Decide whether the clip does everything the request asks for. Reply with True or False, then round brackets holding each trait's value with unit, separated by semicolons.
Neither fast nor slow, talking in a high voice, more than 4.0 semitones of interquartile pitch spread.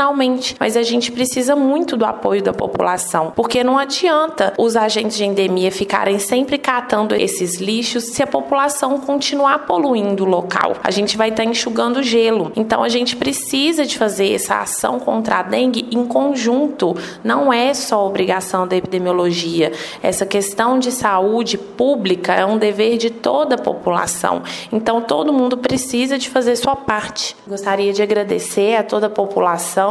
True (160 wpm; 230 Hz; 4.6 semitones)